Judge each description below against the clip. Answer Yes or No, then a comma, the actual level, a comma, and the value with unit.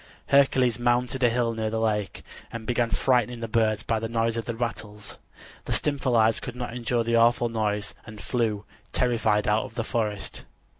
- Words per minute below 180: No, average, 185 wpm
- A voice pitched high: No, low, 115 Hz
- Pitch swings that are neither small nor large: No, narrow, 1.8 semitones